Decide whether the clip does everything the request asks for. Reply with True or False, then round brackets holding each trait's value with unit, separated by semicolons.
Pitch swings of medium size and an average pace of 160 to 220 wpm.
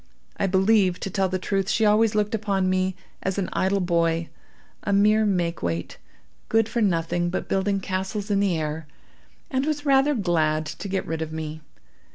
True (3.6 semitones; 185 wpm)